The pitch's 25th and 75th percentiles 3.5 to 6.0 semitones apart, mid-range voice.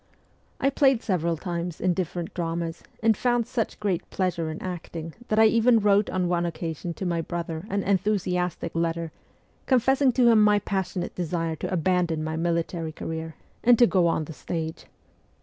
Yes: average, 3.9 semitones; medium, 175 Hz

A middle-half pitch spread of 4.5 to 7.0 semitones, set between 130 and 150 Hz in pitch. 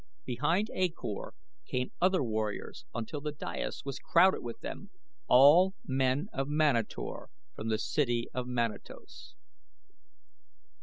Yes: wide, 5.5 semitones; low, 135 Hz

